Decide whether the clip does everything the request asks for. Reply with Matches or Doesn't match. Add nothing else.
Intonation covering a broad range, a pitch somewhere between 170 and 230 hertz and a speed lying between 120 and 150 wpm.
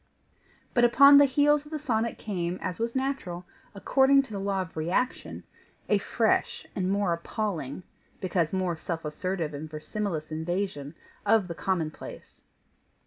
Matches